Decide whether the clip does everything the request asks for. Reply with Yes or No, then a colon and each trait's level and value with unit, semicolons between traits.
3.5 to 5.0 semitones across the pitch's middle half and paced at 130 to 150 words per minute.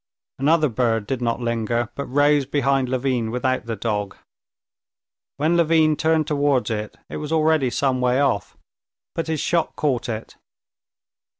Yes: average, 4.3 semitones; average, 145 wpm